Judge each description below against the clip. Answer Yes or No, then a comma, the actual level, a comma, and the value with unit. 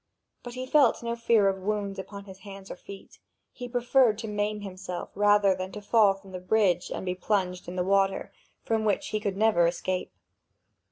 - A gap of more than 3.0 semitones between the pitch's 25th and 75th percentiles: No, narrow, 2.5 semitones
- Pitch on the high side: Yes, high, 200 Hz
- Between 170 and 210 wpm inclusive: Yes, average, 200 wpm